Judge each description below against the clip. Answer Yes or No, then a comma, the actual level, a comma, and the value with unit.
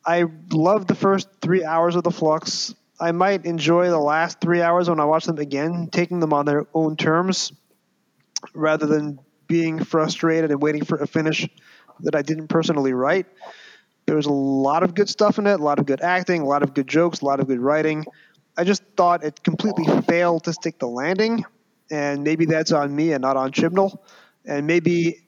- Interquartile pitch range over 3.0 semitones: No, narrow, 2.6 semitones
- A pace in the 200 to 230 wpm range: Yes, fast, 205 wpm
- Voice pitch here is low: No, medium, 165 Hz